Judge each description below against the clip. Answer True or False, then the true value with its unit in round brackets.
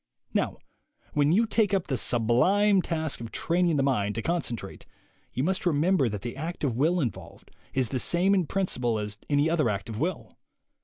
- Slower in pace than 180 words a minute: False (195 wpm)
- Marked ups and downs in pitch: True (6.9 semitones)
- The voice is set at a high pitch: False (150 Hz)